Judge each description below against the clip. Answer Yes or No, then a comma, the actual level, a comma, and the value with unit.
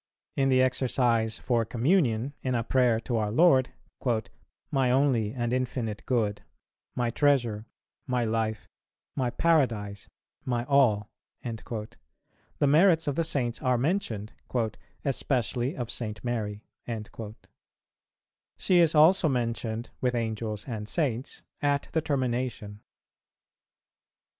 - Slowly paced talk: Yes, slow, 115 wpm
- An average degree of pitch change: Yes, average, 3.5 semitones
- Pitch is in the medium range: No, low, 125 Hz